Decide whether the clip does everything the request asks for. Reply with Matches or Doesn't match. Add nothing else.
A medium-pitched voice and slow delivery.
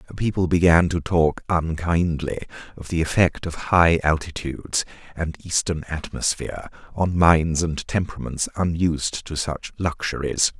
Doesn't match